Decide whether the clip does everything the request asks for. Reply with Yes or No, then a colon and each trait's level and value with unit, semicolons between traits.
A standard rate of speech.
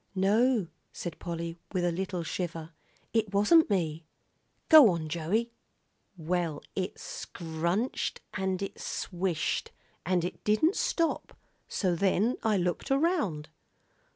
No: slow, 120 wpm